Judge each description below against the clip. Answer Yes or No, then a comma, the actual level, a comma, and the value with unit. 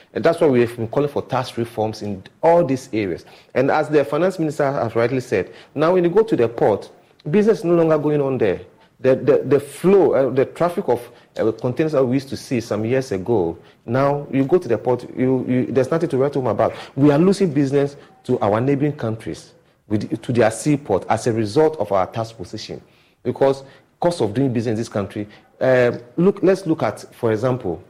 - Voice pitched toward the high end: No, low, 130 Hz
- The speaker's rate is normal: No, fast, 220 wpm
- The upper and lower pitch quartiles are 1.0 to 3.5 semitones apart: No, average, 4.6 semitones